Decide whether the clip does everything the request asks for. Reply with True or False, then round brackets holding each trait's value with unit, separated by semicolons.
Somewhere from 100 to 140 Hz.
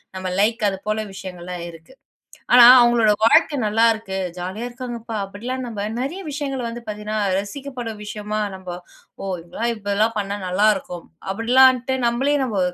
False (220 Hz)